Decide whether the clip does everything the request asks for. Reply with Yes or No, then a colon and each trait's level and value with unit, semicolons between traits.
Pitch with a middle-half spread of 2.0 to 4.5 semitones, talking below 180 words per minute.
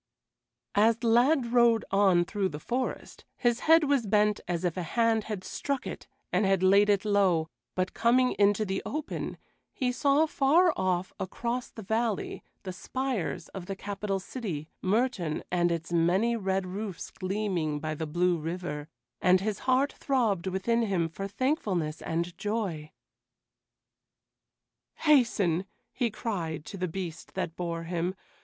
No: average, 4.9 semitones; average, 150 wpm